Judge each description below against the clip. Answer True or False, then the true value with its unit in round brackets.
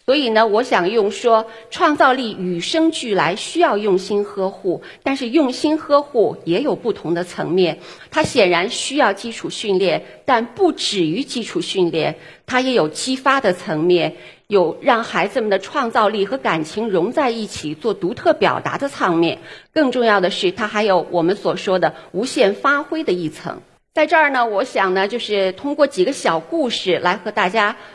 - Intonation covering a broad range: True (7.2 semitones)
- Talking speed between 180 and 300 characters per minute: True (260 characters per minute)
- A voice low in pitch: False (215 Hz)